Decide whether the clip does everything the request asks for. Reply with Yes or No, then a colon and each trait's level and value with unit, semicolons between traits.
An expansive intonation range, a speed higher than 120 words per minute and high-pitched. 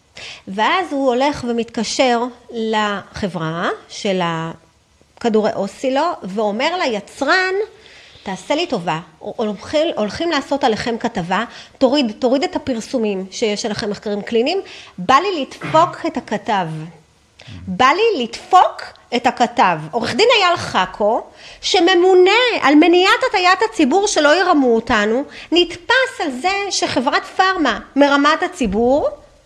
No: wide, 8.3 semitones; average, 115 wpm; very high, 260 Hz